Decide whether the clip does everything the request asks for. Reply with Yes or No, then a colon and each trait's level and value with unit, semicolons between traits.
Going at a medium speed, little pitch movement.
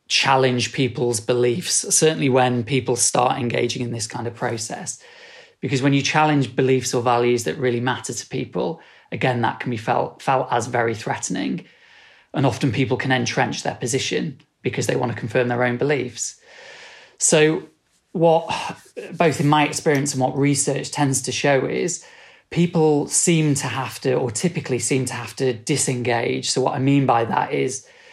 No: average, 175 wpm; average, 3.7 semitones